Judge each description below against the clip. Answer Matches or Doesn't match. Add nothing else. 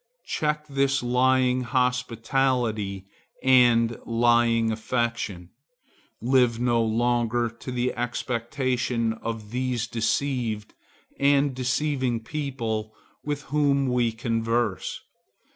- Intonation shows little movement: Matches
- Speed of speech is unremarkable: Doesn't match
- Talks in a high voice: Doesn't match